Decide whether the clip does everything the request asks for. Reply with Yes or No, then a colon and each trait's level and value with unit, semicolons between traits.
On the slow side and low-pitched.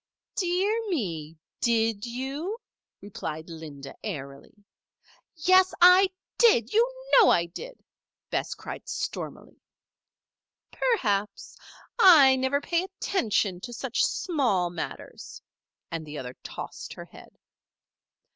No: slow, 105 wpm; high, 240 Hz